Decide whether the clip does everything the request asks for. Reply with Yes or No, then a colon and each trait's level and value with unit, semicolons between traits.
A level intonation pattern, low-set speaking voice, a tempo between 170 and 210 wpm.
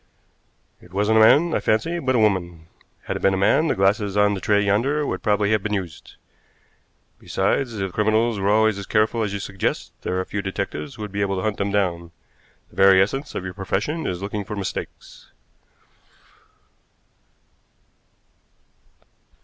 Yes: narrow, 2.1 semitones; low, 100 Hz; average, 175 wpm